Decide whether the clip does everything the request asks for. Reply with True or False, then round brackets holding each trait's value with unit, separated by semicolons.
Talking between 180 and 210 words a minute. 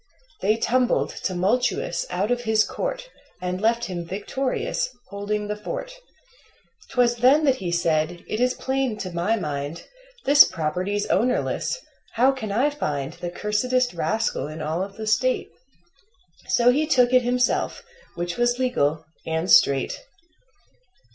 False (140 wpm)